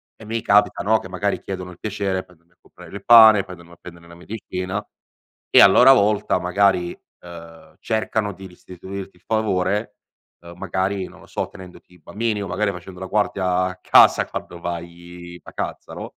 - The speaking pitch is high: No, very low, 95 Hz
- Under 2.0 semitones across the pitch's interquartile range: No, average, 2.7 semitones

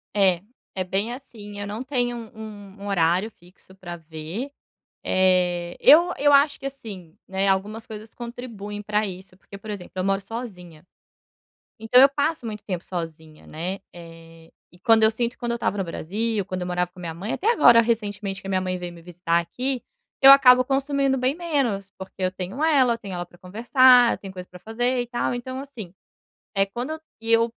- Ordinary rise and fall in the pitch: Yes, average, 5.0 semitones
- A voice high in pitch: Yes, high, 205 Hz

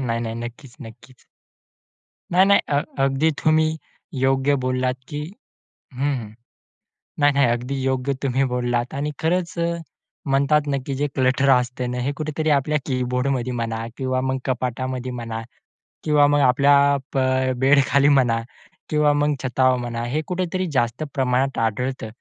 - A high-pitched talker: No, low, 130 Hz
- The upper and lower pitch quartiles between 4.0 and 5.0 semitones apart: No, narrow, 2.6 semitones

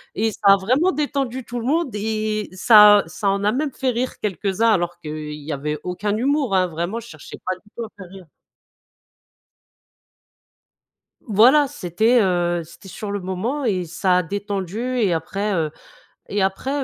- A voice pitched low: No, high, 205 Hz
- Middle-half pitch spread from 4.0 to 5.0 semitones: Yes, average, 4.7 semitones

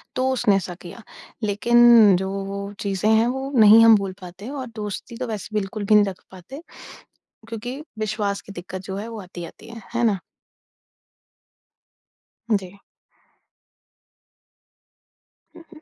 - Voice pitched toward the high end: Yes, high, 210 Hz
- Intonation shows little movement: No, average, 3.1 semitones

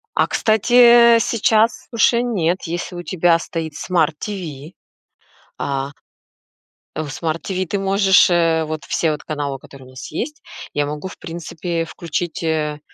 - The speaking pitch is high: No, medium, 170 Hz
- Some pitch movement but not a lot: Yes, average, 4.2 semitones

